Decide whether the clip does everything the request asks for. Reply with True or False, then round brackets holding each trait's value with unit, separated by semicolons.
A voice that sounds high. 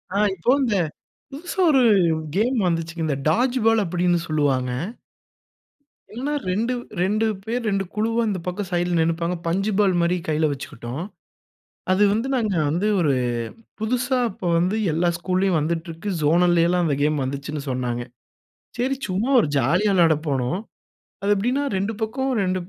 False (180 Hz)